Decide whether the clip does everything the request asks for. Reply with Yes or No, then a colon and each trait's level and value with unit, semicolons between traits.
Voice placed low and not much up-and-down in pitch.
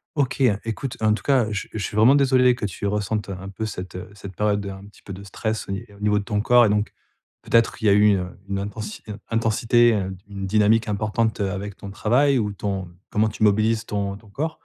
Yes: low, 105 Hz; narrow, 2.2 semitones